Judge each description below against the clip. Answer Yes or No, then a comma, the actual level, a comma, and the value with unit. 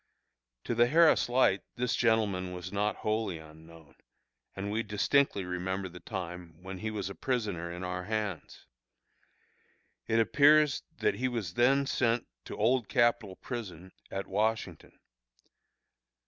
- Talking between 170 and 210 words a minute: No, slow, 135 wpm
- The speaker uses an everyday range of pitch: Yes, average, 4.6 semitones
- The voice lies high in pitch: No, low, 105 Hz